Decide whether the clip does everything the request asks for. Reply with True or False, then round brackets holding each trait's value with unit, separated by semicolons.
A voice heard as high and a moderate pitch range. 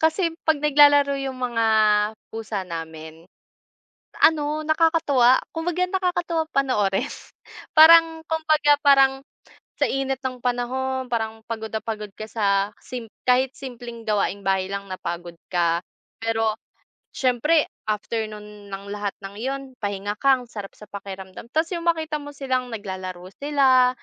False (245 Hz; 6.1 semitones)